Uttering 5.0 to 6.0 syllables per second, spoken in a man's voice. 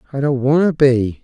Yes: 5.2 syllables/s; male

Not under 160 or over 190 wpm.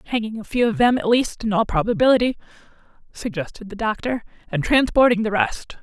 Yes: average, 175 wpm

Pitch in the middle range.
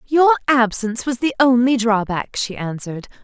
No: high, 240 Hz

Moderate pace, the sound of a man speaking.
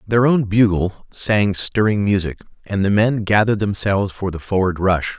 Yes: average, 175 wpm; male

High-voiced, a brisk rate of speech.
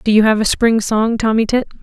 Yes: high, 220 Hz; fast, 265 wpm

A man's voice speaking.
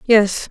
No: female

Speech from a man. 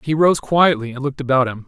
Yes: male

